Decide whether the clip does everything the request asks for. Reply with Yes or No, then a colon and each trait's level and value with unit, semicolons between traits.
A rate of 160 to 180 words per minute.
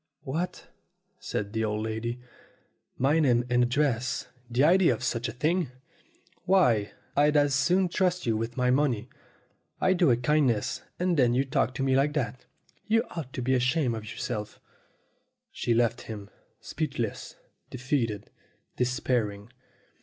No: average, 150 wpm